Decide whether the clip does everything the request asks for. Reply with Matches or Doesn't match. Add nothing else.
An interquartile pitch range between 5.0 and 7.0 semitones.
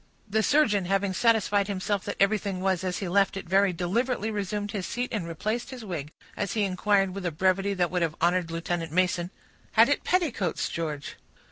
Doesn't match